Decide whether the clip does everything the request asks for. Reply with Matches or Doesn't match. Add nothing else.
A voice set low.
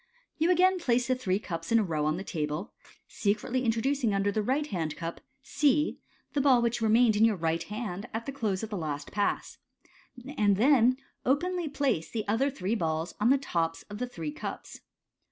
Doesn't match